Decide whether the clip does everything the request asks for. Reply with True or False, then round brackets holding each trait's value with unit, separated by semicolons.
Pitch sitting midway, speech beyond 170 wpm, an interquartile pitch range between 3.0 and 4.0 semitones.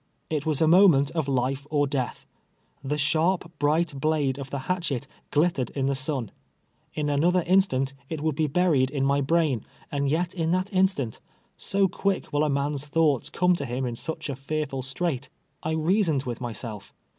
True (145 Hz; 190 wpm; 3.6 semitones)